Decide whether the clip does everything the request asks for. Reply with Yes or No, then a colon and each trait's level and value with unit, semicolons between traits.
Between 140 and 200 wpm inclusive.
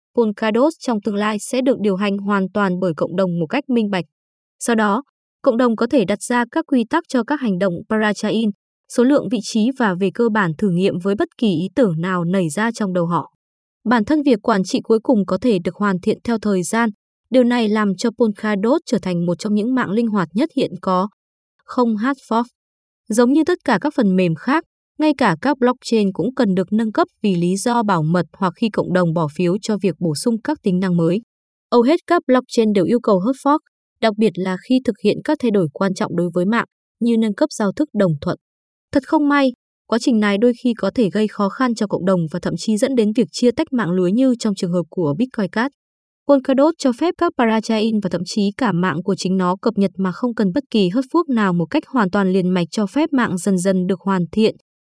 No: average, 245 wpm